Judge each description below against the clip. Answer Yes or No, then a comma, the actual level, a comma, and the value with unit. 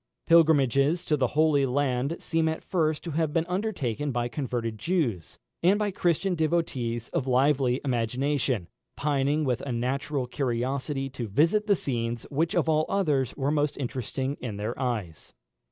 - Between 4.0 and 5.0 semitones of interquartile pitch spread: Yes, average, 4.3 semitones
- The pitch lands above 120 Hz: Yes, medium, 140 Hz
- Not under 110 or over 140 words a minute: No, average, 155 wpm